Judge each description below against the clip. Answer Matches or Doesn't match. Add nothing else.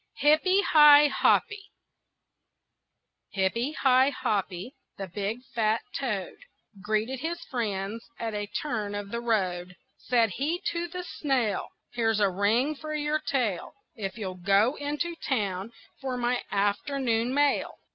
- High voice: Matches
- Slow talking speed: Matches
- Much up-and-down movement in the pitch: Matches